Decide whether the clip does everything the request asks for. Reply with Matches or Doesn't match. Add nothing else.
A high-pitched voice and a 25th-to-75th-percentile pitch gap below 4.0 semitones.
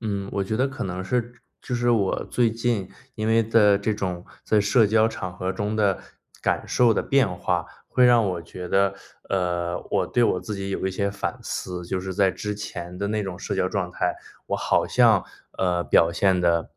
Doesn't match